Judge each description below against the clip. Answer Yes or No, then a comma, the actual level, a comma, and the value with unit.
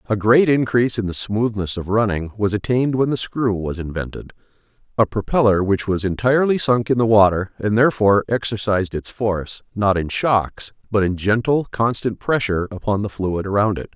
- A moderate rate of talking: Yes, average, 175 wpm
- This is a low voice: Yes, low, 105 Hz